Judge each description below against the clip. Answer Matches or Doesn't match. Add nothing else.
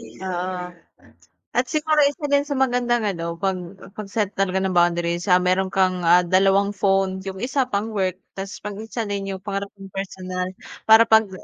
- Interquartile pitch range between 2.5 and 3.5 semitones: Matches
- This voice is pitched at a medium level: Doesn't match